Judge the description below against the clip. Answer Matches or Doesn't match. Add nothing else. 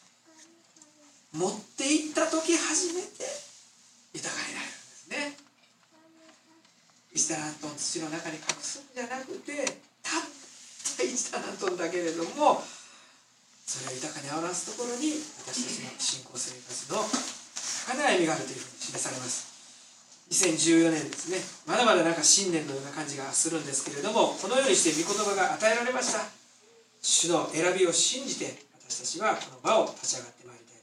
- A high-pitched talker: Matches